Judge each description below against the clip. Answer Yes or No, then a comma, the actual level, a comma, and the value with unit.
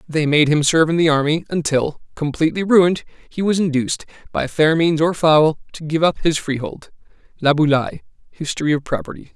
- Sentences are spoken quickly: No, average, 165 wpm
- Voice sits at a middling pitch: Yes, medium, 155 Hz